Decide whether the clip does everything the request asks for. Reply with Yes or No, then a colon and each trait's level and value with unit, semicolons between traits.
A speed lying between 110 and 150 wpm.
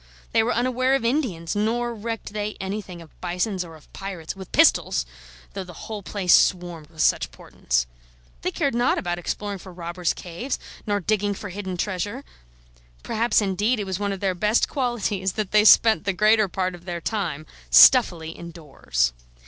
No: average, 175 wpm